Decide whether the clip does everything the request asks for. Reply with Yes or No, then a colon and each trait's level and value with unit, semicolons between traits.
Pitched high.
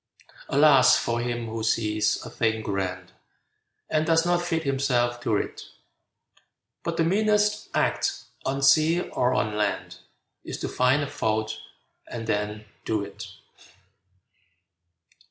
No: low, 120 Hz